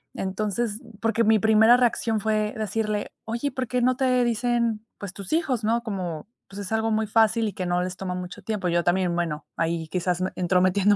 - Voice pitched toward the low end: No, high, 215 Hz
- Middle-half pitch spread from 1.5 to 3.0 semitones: No, average, 3.8 semitones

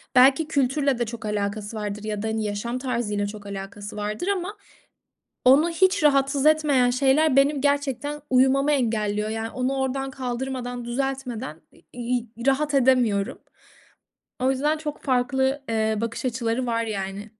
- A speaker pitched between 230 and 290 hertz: Yes, very high, 250 Hz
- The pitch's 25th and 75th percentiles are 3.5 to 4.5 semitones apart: Yes, average, 3.9 semitones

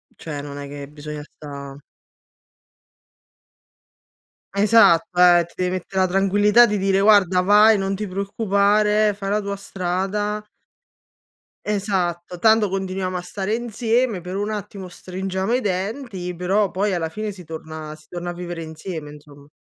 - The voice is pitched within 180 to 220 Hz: Yes, high, 190 Hz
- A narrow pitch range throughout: No, average, 3.0 semitones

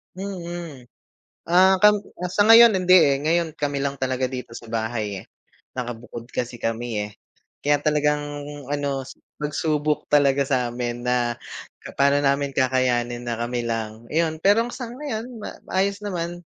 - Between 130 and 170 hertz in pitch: Yes, medium, 140 Hz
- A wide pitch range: Yes, wide, 6.1 semitones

